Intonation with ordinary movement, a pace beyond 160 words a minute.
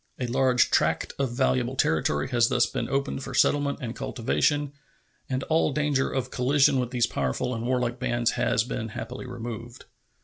No: narrow, 2.2 semitones; average, 170 wpm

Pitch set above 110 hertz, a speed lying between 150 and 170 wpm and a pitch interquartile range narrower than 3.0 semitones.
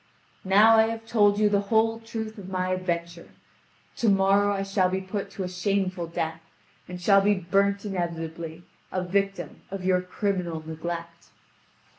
Yes: high, 190 Hz; average, 160 wpm; narrow, 2.6 semitones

